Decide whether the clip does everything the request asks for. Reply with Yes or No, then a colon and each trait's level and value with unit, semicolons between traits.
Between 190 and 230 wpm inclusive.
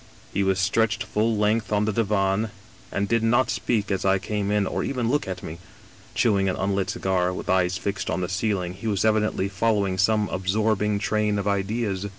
Yes: average, 195 wpm